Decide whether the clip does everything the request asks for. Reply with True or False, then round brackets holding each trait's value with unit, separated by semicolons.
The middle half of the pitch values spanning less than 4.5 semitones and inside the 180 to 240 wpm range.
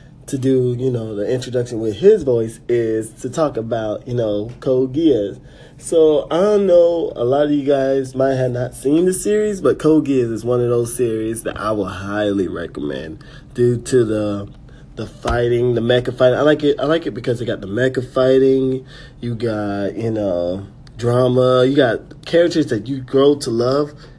True (3.7 semitones; 190 wpm)